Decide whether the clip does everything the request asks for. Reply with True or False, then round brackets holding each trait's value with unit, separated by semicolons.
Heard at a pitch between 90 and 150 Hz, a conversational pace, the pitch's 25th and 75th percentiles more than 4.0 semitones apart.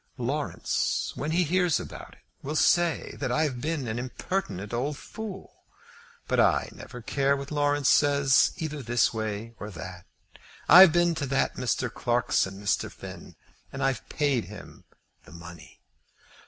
True (135 Hz; 150 wpm; 5.1 semitones)